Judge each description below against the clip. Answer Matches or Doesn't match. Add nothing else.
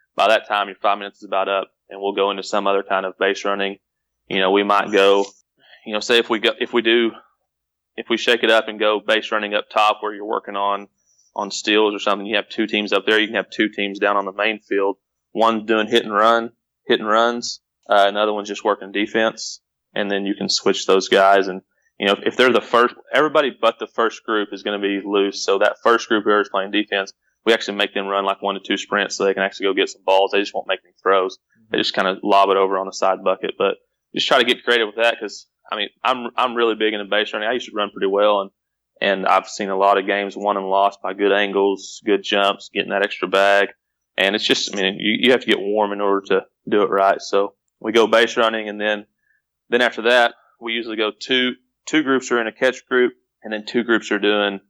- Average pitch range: Doesn't match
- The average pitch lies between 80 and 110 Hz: Matches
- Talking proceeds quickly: Matches